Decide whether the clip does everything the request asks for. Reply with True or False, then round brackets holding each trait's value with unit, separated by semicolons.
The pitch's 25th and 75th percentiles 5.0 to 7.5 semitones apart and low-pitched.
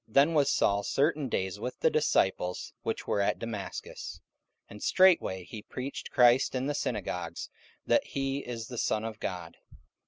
True (5.4 semitones; 115 Hz)